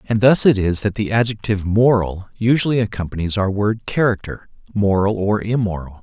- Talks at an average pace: Yes, average, 150 wpm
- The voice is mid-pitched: No, low, 105 Hz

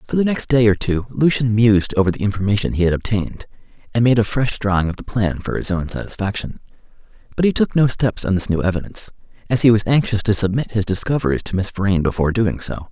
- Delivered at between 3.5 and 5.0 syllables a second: No, 6.3 syllables/s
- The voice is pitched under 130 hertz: Yes, low, 105 Hz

